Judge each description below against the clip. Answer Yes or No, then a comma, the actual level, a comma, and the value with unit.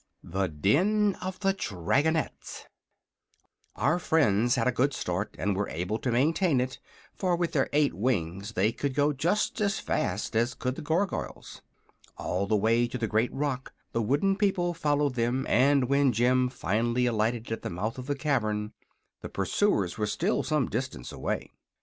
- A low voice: Yes, low, 125 Hz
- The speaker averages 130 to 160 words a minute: No, average, 170 wpm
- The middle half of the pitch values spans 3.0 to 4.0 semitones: No, wide, 5.5 semitones